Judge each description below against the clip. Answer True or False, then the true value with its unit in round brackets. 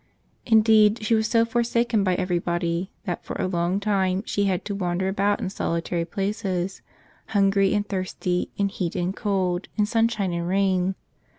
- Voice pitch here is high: True (195 Hz)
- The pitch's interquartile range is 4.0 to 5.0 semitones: False (2.6 semitones)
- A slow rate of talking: False (165 wpm)